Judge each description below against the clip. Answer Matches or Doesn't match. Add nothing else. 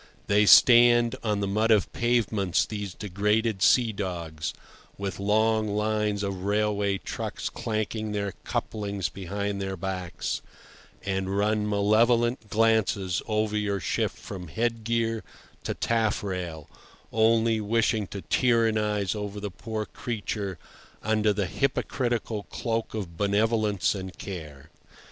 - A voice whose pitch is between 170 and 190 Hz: Doesn't match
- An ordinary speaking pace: Doesn't match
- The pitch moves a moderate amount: Doesn't match